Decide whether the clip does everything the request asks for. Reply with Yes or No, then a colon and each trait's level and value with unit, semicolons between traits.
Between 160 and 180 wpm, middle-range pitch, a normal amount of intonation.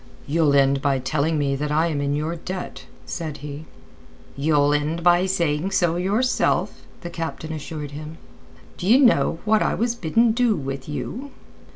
Yes: average, 165 wpm; medium, 160 Hz; average, 3.9 semitones